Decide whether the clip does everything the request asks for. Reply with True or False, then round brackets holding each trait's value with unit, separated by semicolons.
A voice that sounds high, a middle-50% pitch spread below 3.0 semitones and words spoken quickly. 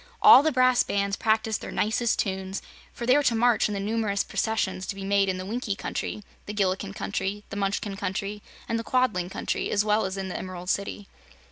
True (205 Hz; 2.4 semitones; 215 wpm)